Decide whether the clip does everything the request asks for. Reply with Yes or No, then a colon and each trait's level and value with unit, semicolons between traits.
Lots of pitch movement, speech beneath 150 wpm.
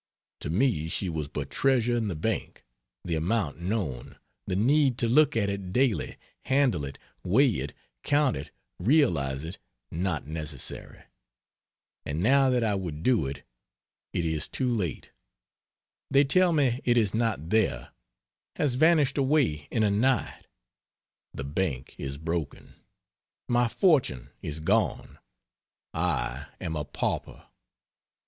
Yes: wide, 8.6 semitones; average, 140 wpm